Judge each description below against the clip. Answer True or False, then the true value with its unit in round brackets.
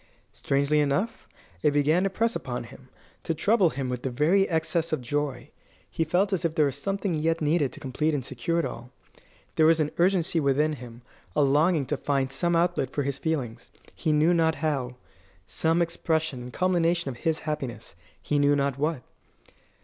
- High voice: False (155 Hz)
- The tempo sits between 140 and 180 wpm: False (190 wpm)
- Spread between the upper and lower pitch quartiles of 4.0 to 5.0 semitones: False (3.5 semitones)